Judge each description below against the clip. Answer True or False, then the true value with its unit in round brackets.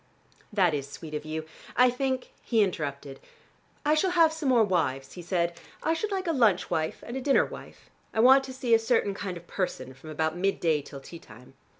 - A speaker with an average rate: False (225 wpm)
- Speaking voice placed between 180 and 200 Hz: True (190 Hz)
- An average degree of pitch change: False (8.6 semitones)